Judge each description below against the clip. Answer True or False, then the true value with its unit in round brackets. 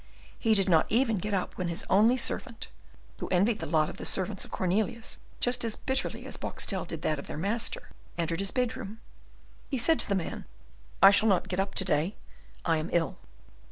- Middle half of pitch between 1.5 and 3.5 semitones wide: False (4.5 semitones)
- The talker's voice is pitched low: False (195 Hz)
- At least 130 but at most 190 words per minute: False (205 wpm)